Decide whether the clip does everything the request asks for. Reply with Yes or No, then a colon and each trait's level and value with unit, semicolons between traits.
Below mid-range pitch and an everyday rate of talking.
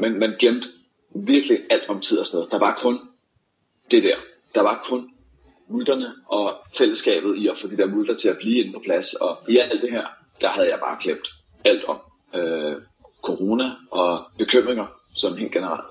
No: very high, 250 Hz; average, 190 wpm